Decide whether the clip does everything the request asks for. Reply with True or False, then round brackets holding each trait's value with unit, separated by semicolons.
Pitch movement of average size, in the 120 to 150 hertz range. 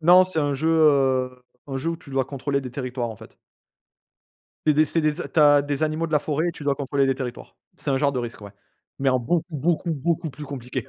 True (3.0 semitones; 140 Hz)